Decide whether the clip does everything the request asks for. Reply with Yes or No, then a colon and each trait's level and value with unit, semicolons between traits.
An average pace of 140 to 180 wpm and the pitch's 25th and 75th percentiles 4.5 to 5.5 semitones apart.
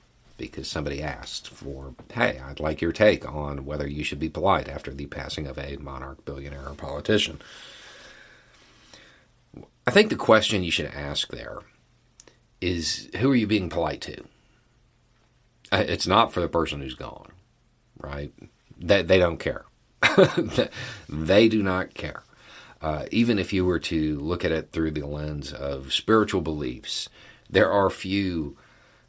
Yes: average, 150 wpm; average, 4.9 semitones